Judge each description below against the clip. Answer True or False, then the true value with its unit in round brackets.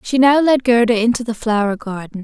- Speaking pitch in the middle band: False (230 Hz)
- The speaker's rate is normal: False (215 wpm)